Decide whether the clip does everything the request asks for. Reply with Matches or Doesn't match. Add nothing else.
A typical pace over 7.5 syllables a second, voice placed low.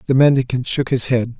Doesn't match